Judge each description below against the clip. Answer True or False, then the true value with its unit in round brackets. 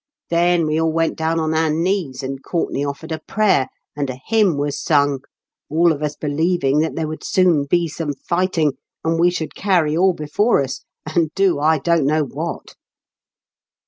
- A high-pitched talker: False (160 Hz)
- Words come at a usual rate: True (180 wpm)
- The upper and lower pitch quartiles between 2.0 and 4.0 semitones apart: True (2.8 semitones)